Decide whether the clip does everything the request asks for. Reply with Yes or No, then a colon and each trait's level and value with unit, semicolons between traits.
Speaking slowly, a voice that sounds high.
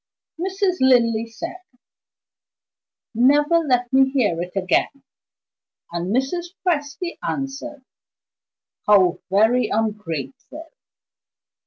Yes: slow, 80 wpm; very high, 260 Hz